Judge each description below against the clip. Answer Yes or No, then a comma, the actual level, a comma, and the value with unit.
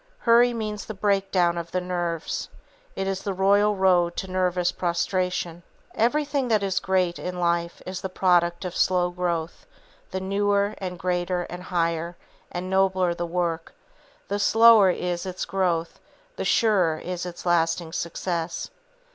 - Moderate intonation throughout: No, narrow, 2.0 semitones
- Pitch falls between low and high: Yes, medium, 180 Hz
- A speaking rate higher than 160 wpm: No, average, 150 wpm